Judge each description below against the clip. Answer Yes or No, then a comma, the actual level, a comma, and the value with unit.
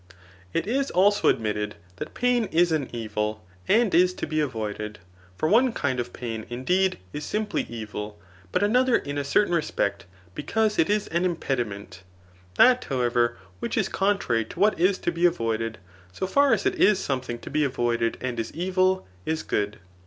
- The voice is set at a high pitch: No, medium, 150 Hz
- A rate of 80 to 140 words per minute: No, average, 175 wpm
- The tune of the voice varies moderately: No, wide, 8.8 semitones